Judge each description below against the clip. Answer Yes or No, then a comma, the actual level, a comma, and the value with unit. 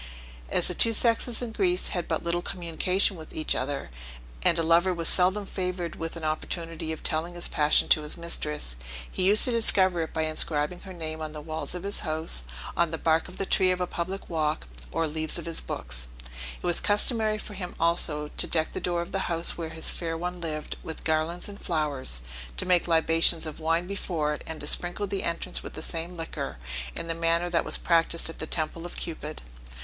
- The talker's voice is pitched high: No, medium, 165 Hz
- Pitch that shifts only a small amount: Yes, narrow, 2.2 semitones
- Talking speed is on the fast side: Yes, fast, 215 wpm